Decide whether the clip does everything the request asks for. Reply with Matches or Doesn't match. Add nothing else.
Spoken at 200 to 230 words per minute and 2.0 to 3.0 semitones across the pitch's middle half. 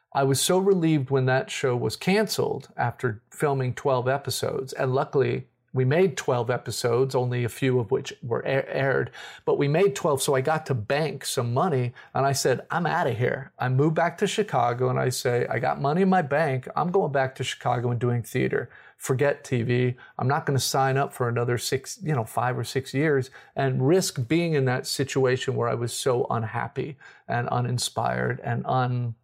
Matches